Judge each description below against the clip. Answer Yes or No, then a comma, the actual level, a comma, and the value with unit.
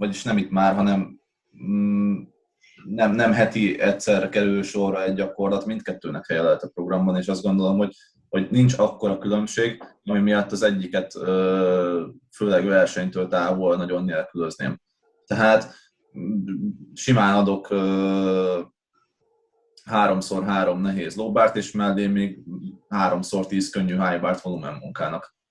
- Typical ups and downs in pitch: No, narrow, 1.6 semitones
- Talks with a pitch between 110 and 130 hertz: No, very low, 95 Hz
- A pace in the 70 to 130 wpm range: Yes, average, 125 wpm